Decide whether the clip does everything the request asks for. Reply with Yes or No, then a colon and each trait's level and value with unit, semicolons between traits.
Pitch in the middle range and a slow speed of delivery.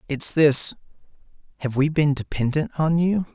Yes: medium, 150 Hz; slow, 125 wpm